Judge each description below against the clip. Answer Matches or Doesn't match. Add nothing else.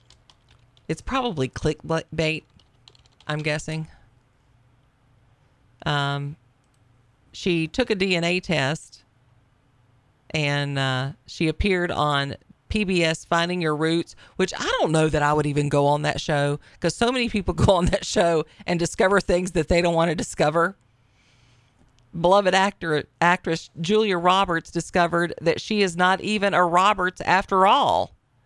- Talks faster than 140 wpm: Doesn't match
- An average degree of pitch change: Doesn't match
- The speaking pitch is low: Doesn't match